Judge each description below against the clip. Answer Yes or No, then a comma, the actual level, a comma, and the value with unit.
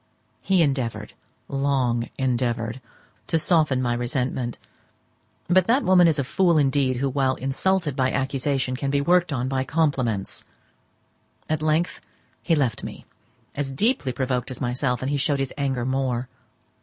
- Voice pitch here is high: No, low, 135 Hz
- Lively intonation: No, average, 3.2 semitones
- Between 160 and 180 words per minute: No, average, 150 wpm